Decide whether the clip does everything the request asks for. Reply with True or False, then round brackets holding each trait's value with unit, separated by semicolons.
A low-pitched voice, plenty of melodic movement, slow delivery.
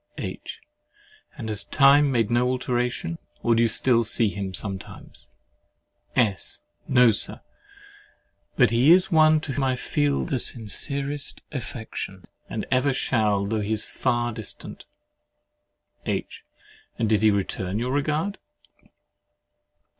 False (120 Hz; 4.3 semitones; 130 wpm)